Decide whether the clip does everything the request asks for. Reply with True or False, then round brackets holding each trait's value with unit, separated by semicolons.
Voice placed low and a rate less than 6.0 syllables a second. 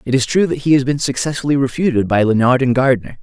False (130 Hz; 6.4 syllables/s)